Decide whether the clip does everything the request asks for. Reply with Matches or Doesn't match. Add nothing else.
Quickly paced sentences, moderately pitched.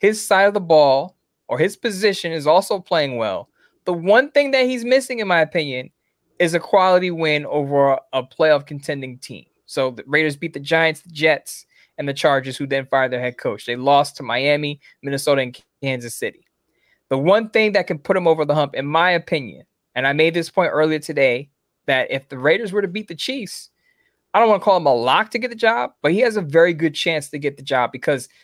Matches